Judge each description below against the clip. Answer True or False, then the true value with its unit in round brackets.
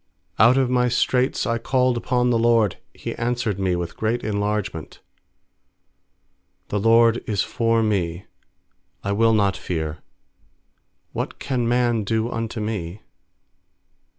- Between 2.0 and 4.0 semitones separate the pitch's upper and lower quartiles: True (2.9 semitones)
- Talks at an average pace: False (130 wpm)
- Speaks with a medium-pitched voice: False (115 Hz)